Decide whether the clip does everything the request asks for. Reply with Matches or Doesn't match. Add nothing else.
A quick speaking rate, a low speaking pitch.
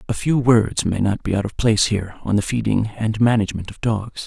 Matches